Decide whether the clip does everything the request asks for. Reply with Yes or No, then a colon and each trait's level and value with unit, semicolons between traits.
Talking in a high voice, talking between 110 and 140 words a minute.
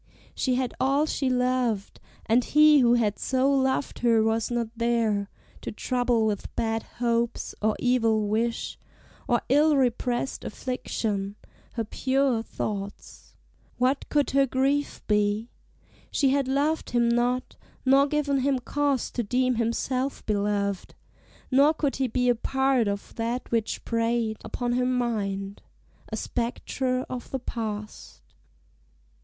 Yes: high, 245 Hz; slow, 135 wpm